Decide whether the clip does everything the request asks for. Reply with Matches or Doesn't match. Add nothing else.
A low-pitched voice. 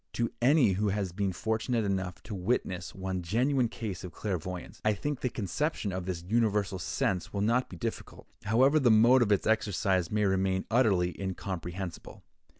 Matches